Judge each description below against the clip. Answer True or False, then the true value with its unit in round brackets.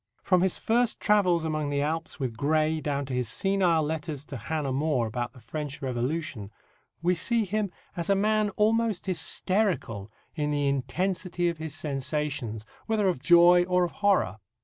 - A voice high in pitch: False (160 Hz)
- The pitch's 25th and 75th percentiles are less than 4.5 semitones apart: False (4.9 semitones)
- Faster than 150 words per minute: True (170 wpm)